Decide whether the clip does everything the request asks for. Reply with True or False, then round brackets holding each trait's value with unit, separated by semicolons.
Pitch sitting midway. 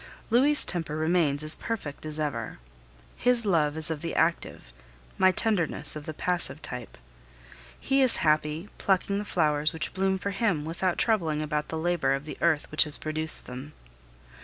True (160 Hz)